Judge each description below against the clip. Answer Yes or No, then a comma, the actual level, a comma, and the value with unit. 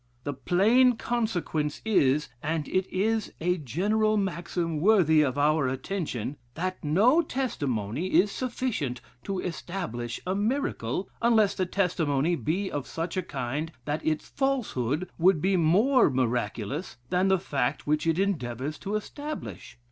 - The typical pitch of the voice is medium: Yes, medium, 175 Hz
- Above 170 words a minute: No, average, 140 wpm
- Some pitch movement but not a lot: No, wide, 5.8 semitones